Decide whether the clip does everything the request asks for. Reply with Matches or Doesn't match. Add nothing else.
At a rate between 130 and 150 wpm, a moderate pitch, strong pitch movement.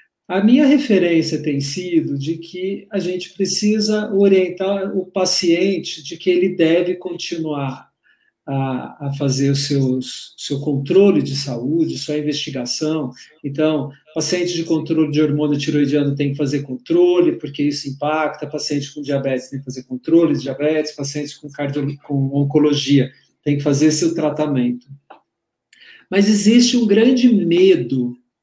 Doesn't match